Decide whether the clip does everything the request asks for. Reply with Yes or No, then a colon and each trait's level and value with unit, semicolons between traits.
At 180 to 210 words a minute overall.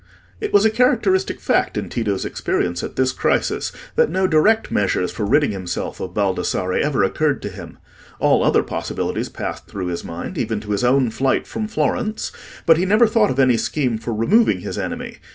Yes: average, 190 wpm